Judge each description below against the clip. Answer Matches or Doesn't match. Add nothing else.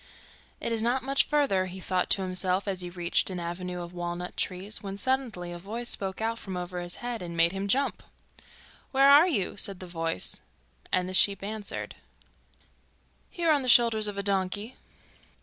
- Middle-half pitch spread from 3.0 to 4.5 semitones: Matches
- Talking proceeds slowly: Doesn't match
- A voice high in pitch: Matches